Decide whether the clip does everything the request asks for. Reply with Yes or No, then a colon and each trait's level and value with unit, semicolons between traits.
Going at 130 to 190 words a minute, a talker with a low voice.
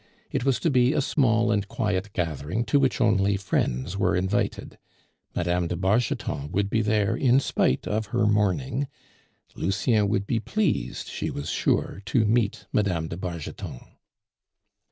Yes: average, 155 wpm; low, 105 Hz